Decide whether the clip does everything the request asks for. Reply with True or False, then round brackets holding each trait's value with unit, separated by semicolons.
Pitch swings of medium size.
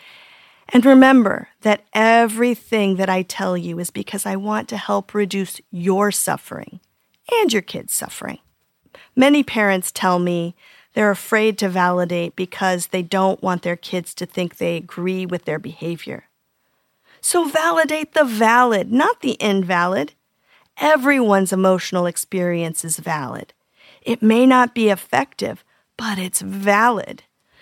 True (4.3 semitones)